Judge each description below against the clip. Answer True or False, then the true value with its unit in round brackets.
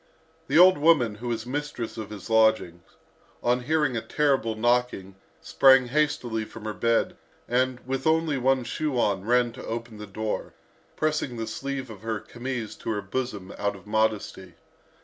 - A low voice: True (120 Hz)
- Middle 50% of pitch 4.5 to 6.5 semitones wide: False (3.5 semitones)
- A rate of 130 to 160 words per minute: False (170 wpm)